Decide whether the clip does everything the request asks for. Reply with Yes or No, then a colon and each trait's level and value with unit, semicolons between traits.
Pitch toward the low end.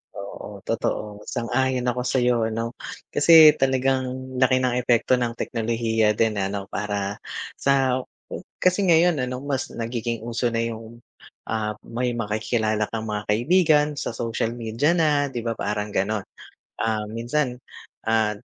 Yes: low, 120 Hz